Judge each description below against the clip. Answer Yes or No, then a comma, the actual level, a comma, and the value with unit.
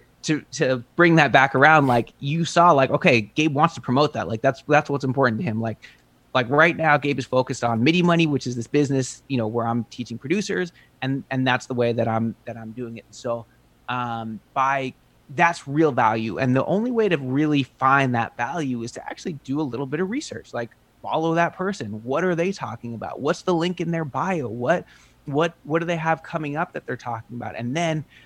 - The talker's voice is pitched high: No, low, 135 Hz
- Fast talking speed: Yes, fast, 225 wpm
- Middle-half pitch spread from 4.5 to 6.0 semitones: Yes, average, 5.3 semitones